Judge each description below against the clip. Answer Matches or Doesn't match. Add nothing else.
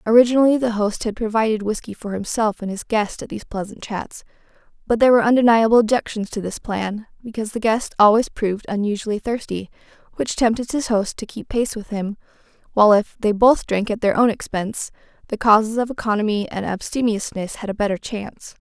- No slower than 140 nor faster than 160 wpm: Doesn't match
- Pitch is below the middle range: Doesn't match